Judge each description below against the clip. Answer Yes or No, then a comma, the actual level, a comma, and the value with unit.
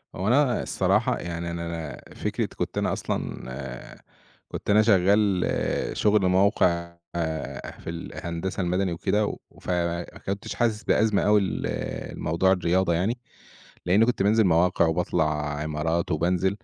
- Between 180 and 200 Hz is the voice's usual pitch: No, very low, 90 Hz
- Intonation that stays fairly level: No, average, 3.2 semitones